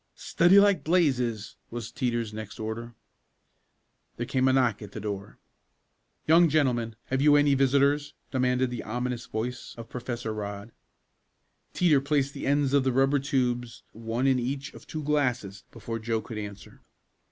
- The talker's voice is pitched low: Yes, low, 125 Hz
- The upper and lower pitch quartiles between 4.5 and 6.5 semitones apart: No, average, 3.6 semitones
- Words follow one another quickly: No, average, 155 wpm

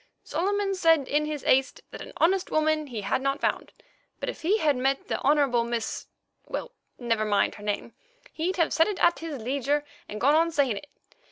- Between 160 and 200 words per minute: Yes, average, 190 wpm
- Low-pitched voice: No, very high, 295 Hz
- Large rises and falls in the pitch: No, average, 4.7 semitones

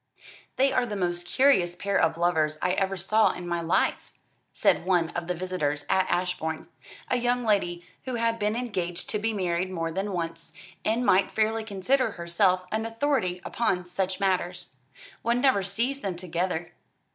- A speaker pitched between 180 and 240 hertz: Yes, medium, 185 Hz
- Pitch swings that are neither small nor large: Yes, average, 4.2 semitones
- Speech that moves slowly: No, average, 170 wpm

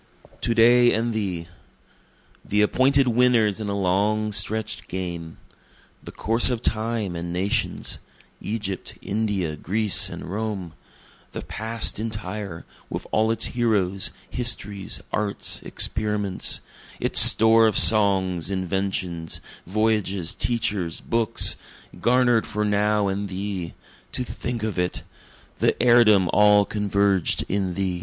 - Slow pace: Yes, slow, 120 wpm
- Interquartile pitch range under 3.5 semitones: Yes, average, 2.8 semitones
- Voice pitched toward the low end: Yes, low, 105 Hz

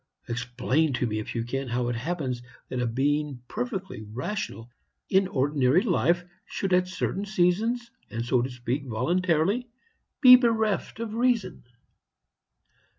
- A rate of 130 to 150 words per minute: Yes, average, 140 wpm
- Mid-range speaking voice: Yes, medium, 155 Hz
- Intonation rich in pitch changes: Yes, wide, 8.1 semitones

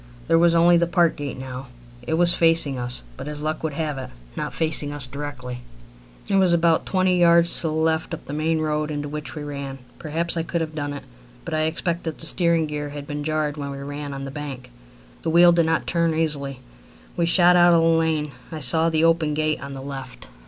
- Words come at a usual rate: No, fast, 230 wpm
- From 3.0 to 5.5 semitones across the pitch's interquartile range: No, narrow, 2.4 semitones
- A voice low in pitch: No, medium, 155 Hz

